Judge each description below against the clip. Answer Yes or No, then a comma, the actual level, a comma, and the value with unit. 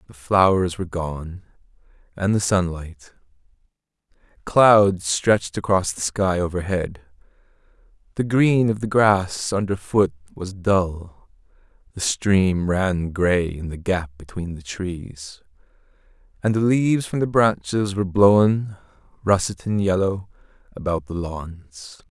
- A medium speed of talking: No, slow, 120 wpm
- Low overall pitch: Yes, very low, 95 Hz